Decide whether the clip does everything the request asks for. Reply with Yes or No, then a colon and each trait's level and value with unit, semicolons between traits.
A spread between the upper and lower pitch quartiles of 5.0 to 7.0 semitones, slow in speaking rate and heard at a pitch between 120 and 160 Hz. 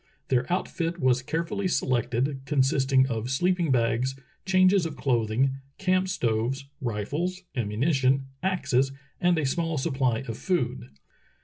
Yes: wide, 5.5 semitones; slow, 125 wpm; low, 135 Hz